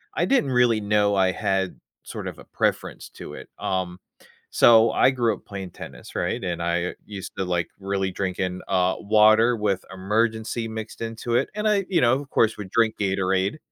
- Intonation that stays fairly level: No, average, 3.5 semitones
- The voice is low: Yes, low, 105 Hz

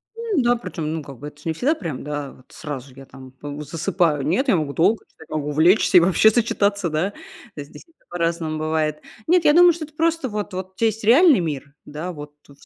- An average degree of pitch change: No, wide, 6.9 semitones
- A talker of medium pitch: Yes, medium, 170 Hz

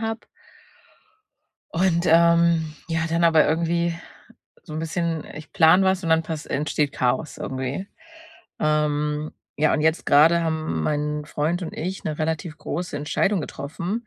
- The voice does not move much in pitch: Yes, narrow, 2.1 semitones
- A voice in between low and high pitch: Yes, medium, 160 Hz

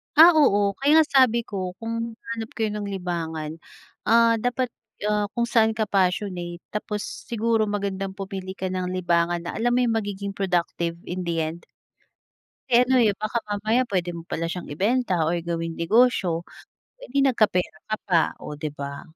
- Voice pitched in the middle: No, high, 200 Hz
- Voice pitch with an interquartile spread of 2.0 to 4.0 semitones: No, average, 4.7 semitones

